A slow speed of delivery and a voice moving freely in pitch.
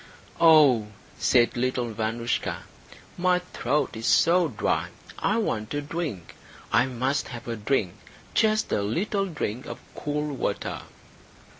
Yes: slow, 130 wpm; wide, 6.0 semitones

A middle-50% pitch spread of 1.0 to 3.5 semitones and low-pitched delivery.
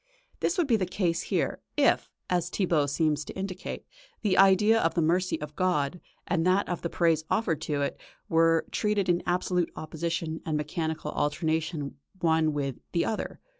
No: average, 2.8 semitones; medium, 165 Hz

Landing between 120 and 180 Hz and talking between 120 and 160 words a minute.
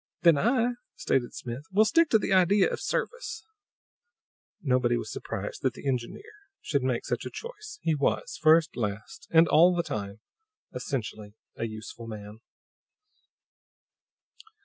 Yes: medium, 140 Hz; average, 140 wpm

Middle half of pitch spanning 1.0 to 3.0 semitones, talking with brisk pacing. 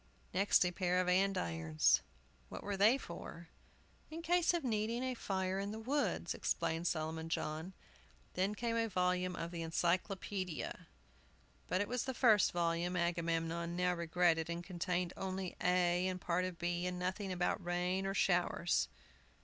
No: narrow, 2.4 semitones; average, 160 wpm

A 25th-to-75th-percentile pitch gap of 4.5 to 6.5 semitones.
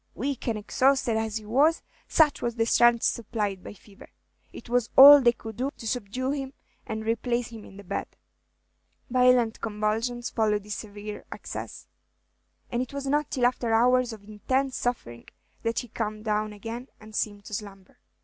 No: average, 2.9 semitones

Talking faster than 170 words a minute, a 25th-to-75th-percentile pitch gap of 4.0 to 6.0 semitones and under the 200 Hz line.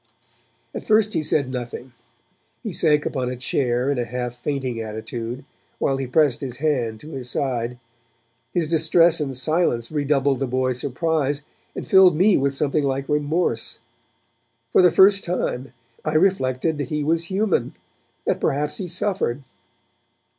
No: average, 155 wpm; average, 4.3 semitones; medium, 140 Hz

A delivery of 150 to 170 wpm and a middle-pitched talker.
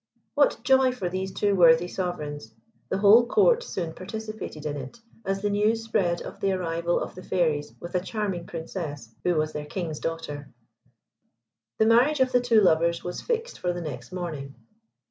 No: average, 180 wpm; medium, 180 Hz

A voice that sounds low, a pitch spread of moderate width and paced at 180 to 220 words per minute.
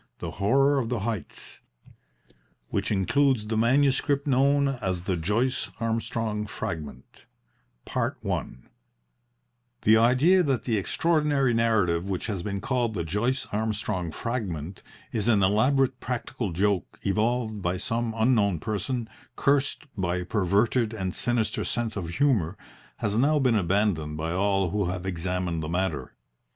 No: low, 105 Hz; average, 5.0 semitones; slow, 135 wpm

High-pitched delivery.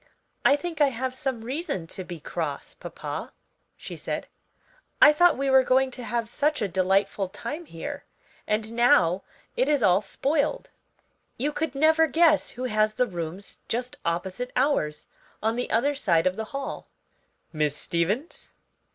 Yes: high, 240 Hz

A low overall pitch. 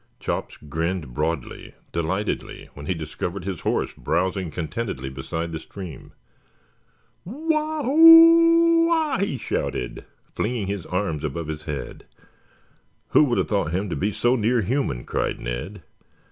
Yes: very low, 95 Hz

